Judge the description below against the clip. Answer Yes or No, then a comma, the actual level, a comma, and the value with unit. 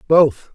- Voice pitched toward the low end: No, medium, 150 Hz